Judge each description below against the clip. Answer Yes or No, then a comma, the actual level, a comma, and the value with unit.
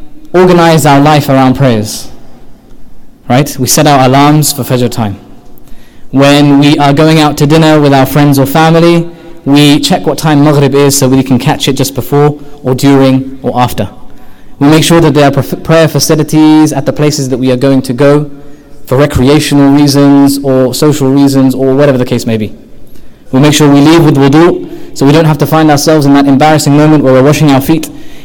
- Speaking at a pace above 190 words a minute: Yes, average, 200 wpm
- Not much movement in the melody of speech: Yes, narrow, 2.2 semitones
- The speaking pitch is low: No, medium, 145 Hz